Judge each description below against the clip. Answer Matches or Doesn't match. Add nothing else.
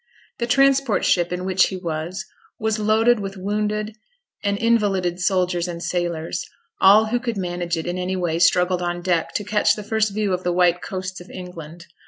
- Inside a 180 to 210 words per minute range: Matches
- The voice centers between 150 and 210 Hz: Matches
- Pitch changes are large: Doesn't match